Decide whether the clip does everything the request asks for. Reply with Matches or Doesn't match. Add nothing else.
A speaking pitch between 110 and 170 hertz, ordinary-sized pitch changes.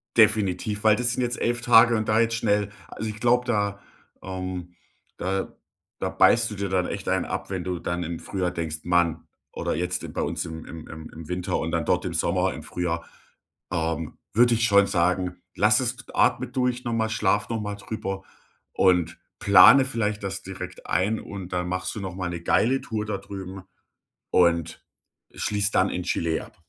Doesn't match